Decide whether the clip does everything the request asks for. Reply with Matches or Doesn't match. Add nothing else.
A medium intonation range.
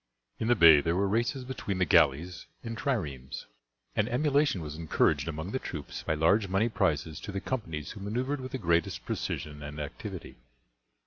Doesn't match